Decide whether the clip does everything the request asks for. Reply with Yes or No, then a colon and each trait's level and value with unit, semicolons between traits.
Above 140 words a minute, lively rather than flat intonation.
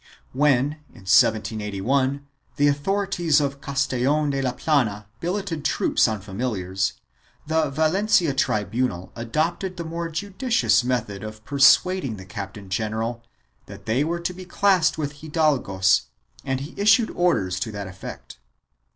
No: slow, 135 wpm; wide, 6.9 semitones